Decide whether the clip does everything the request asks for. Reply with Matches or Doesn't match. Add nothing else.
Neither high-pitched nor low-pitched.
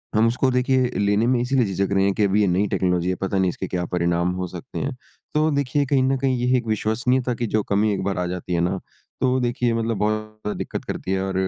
Doesn't match